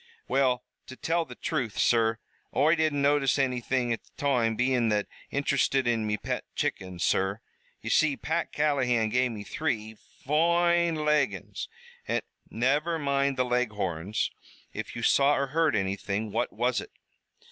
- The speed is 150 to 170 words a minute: Yes, average, 155 wpm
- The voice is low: Yes, low, 130 Hz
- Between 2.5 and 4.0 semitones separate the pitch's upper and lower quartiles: No, average, 4.6 semitones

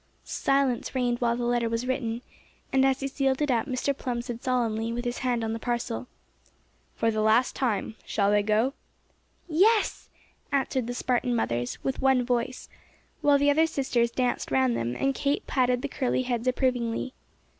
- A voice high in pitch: Yes, high, 245 Hz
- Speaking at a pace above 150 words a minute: Yes, average, 175 wpm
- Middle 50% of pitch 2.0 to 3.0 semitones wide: Yes, narrow, 2.4 semitones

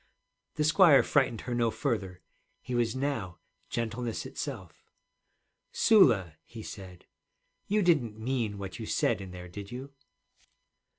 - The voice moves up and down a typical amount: No, wide, 5.8 semitones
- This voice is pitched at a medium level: No, low, 115 Hz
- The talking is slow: Yes, slow, 130 wpm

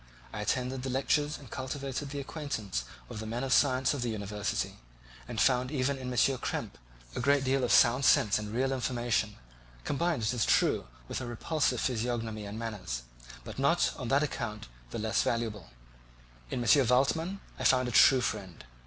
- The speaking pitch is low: Yes, low, 125 Hz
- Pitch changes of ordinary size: Yes, average, 3.6 semitones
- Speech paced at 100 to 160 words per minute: No, average, 185 wpm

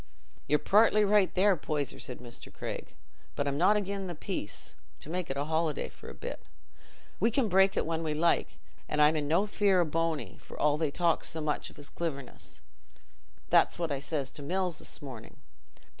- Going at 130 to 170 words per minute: No, average, 190 wpm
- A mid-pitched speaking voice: Yes, medium, 160 Hz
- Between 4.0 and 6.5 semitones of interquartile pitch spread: Yes, average, 4.5 semitones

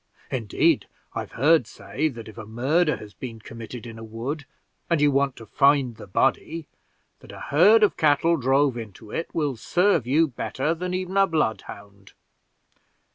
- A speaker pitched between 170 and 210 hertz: No, low, 135 Hz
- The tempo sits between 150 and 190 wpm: Yes, average, 170 wpm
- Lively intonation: Yes, wide, 6.0 semitones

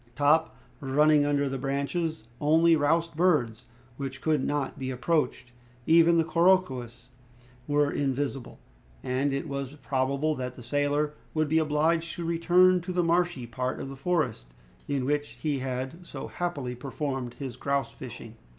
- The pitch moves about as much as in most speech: Yes, average, 3.6 semitones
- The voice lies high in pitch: No, medium, 145 Hz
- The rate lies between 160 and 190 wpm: No, average, 150 wpm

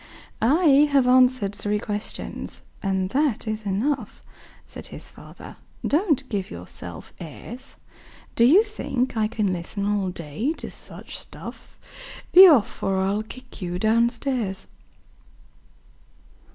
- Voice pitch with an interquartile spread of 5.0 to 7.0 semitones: Yes, wide, 5.4 semitones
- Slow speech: Yes, slow, 125 wpm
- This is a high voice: Yes, high, 220 Hz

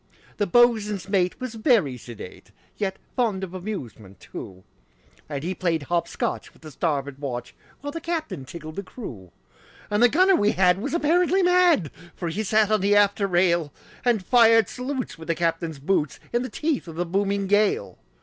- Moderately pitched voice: No, high, 195 Hz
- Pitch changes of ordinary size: No, wide, 6.4 semitones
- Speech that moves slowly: No, average, 180 wpm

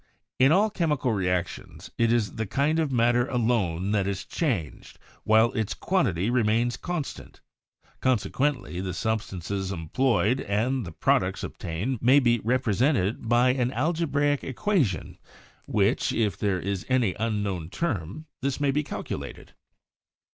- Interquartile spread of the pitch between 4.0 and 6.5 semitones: Yes, average, 5.2 semitones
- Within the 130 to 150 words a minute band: Yes, average, 145 wpm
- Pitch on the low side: Yes, low, 115 Hz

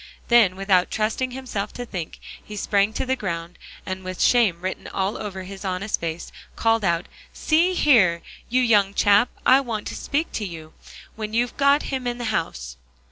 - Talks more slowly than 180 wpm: No, average, 185 wpm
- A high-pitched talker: Yes, high, 210 Hz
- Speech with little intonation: No, average, 4.7 semitones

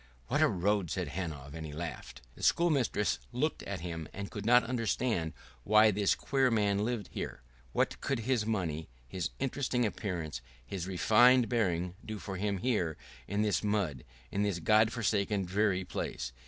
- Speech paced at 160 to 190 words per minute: Yes, average, 170 wpm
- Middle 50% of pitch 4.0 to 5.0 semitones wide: Yes, average, 4.5 semitones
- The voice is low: Yes, low, 100 Hz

